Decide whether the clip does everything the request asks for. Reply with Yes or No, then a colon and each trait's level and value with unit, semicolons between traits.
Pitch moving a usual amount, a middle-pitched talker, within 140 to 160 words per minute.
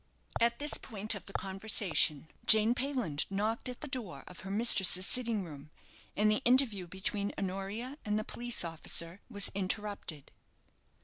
No: average, 3.8 semitones; high, 205 Hz; average, 150 wpm